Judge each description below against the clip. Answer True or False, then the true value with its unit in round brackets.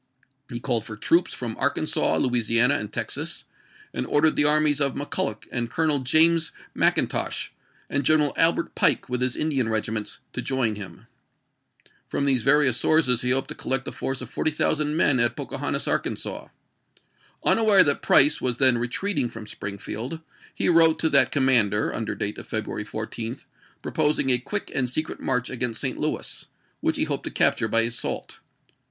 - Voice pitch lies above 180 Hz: False (130 Hz)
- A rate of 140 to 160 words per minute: False (170 wpm)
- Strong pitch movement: False (4.3 semitones)